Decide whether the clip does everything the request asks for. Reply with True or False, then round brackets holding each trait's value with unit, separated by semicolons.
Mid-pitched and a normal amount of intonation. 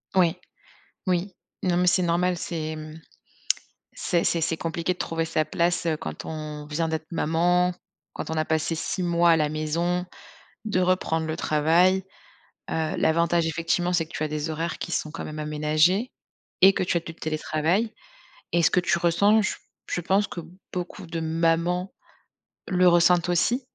False (170 Hz; 2.1 semitones)